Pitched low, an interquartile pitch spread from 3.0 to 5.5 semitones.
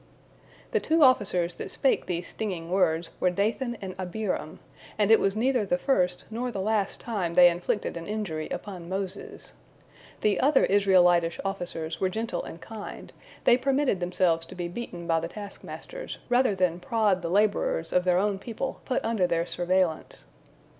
No: high, 190 Hz; average, 3.8 semitones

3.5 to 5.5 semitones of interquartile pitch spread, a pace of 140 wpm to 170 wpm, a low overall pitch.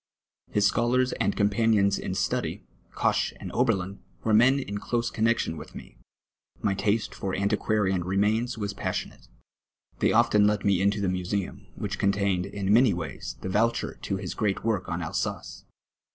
No: narrow, 2.6 semitones; average, 165 wpm; low, 100 Hz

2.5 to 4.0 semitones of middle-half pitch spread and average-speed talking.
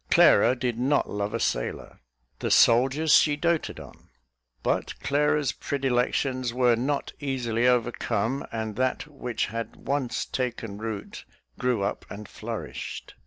No: average, 3.3 semitones; slow, 130 wpm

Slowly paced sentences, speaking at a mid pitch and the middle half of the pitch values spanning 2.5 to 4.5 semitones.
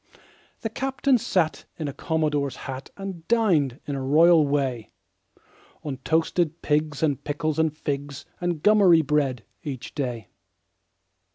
Yes: slow, 130 wpm; medium, 150 Hz; average, 3.5 semitones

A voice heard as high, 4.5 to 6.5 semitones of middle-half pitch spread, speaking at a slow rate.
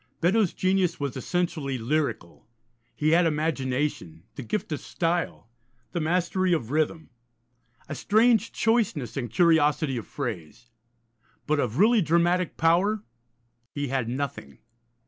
No: medium, 155 Hz; average, 5.0 semitones; slow, 125 wpm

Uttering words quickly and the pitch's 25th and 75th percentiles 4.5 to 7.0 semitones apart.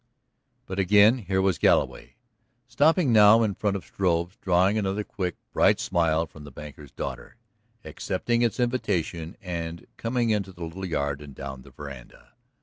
No: average, 155 wpm; average, 4.8 semitones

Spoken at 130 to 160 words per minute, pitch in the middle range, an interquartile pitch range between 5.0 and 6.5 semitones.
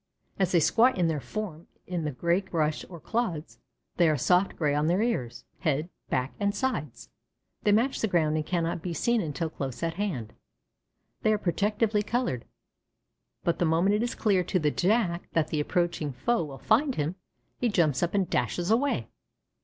No: average, 185 wpm; medium, 175 Hz; average, 5.3 semitones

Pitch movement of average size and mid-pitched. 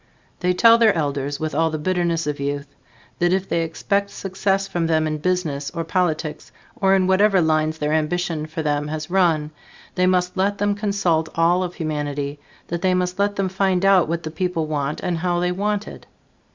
Yes: average, 3.3 semitones; medium, 175 Hz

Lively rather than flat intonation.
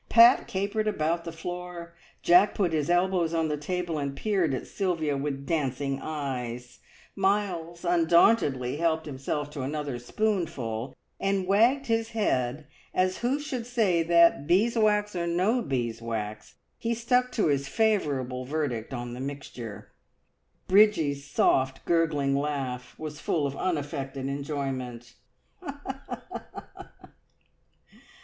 Yes: wide, 5.7 semitones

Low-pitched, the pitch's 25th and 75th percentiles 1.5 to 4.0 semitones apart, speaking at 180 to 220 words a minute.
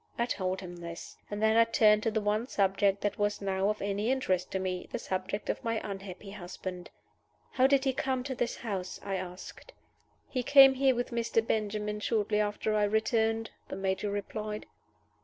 No: high, 210 Hz; average, 2.9 semitones; average, 190 wpm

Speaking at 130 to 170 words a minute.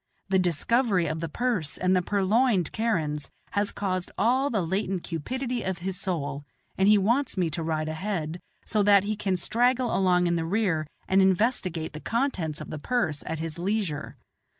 No: average, 180 wpm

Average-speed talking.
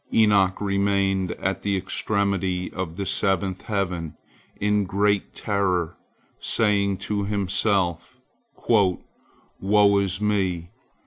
No: slow, 100 wpm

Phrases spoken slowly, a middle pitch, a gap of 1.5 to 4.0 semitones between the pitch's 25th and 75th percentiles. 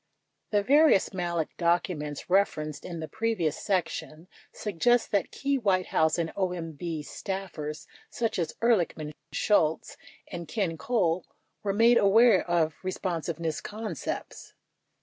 No: slow, 120 wpm; medium, 180 Hz; average, 4.4 semitones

